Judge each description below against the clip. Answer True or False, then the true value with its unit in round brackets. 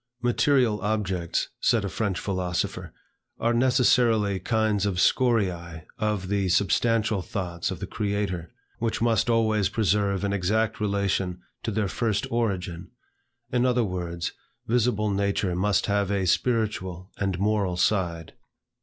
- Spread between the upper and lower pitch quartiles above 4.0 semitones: False (3.2 semitones)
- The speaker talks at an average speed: False (130 wpm)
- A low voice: True (100 Hz)